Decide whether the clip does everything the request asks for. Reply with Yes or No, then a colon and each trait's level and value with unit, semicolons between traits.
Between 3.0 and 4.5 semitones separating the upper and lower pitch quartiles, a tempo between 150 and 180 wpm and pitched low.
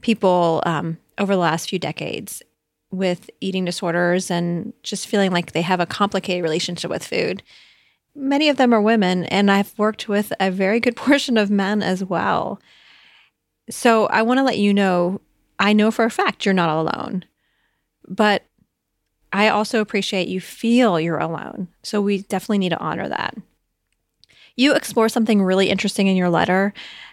No: average, 3.4 semitones; average, 170 wpm; high, 200 Hz